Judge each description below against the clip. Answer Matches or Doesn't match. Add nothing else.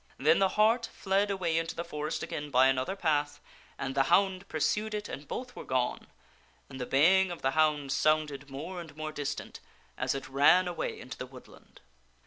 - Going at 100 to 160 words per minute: Doesn't match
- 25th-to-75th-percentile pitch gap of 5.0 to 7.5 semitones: Matches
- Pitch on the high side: Doesn't match